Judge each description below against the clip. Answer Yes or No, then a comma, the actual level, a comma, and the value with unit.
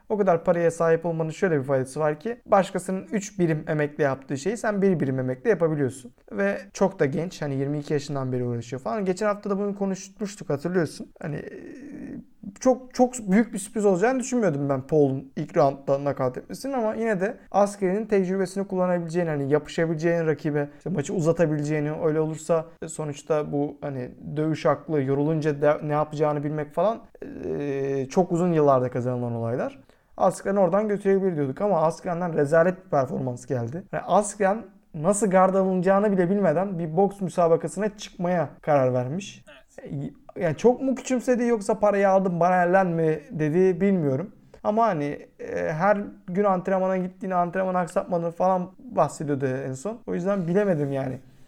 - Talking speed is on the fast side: Yes, fast, 155 wpm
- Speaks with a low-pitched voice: No, medium, 175 Hz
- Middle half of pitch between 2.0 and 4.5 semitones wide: No, average, 5.1 semitones